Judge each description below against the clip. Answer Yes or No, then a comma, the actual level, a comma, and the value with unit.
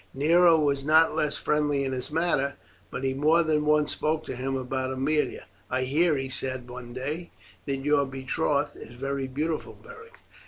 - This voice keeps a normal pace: Yes, average, 180 wpm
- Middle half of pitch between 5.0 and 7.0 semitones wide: No, average, 2.8 semitones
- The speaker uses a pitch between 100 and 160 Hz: Yes, medium, 140 Hz